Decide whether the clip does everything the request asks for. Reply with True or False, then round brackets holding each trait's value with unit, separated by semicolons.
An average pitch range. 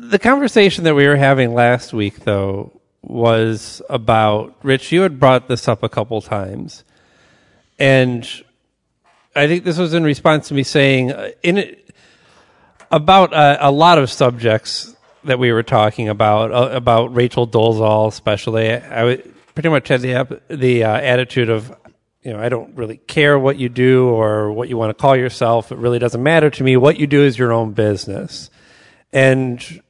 True (4.0 semitones)